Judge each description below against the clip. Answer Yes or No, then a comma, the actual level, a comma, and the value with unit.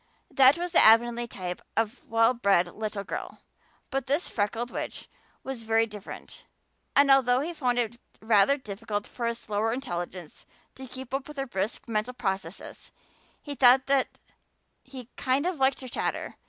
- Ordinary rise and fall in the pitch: Yes, average, 4.0 semitones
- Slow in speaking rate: No, average, 165 wpm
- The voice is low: No, high, 240 Hz